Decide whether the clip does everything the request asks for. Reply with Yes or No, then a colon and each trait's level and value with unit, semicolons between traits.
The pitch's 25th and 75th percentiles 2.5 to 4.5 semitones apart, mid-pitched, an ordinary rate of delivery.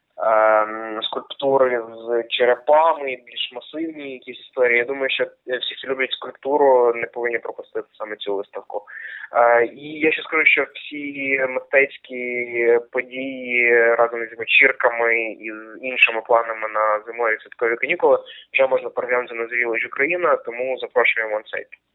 No: average, 4.1 semitones; low, 125 Hz; average, 135 wpm